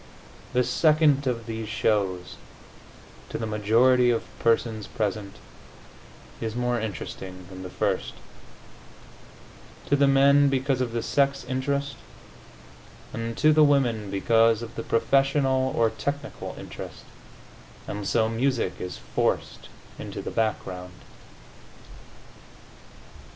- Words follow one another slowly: Yes, slow, 115 wpm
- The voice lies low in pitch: Yes, low, 115 Hz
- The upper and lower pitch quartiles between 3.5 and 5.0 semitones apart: Yes, average, 4.0 semitones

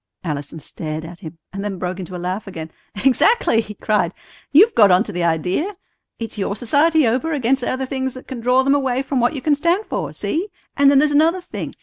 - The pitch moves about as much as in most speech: No, wide, 7.6 semitones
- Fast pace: Yes, fast, 220 wpm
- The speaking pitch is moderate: No, high, 245 Hz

